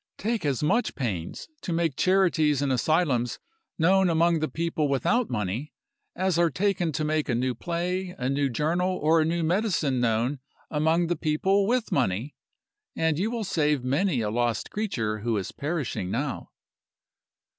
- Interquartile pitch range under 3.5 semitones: No, wide, 5.6 semitones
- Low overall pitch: No, medium, 155 Hz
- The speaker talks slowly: No, average, 165 wpm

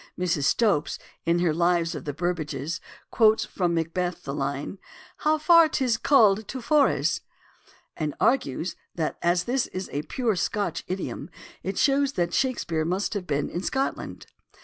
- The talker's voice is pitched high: No, medium, 180 Hz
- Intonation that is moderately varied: No, wide, 6.2 semitones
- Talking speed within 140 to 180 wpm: Yes, average, 160 wpm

